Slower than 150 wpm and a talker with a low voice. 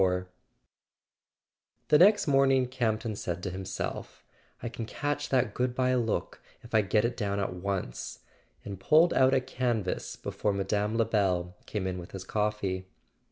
No: average, 160 wpm; low, 110 Hz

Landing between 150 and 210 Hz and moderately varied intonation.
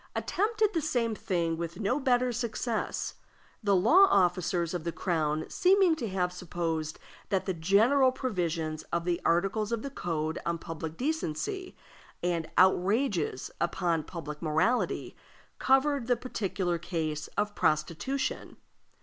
No: medium, 185 Hz; wide, 6.9 semitones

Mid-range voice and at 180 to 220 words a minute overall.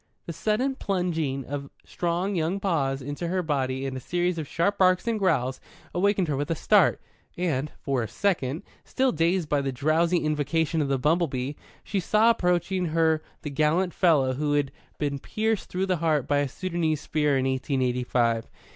Yes: medium, 160 Hz; average, 190 wpm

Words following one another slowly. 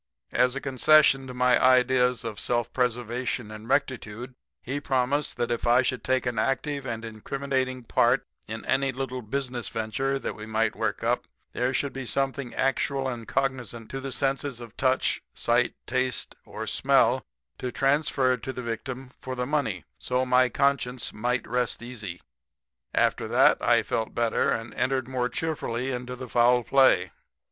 No: average, 165 wpm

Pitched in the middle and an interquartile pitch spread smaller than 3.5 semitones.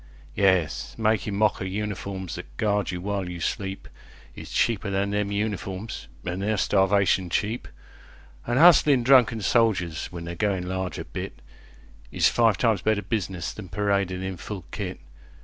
No: low, 100 Hz; average, 2.7 semitones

